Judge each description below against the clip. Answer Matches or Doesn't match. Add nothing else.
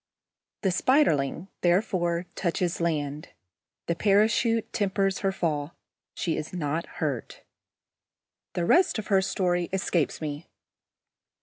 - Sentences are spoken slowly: Matches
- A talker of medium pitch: Matches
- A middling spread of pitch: Matches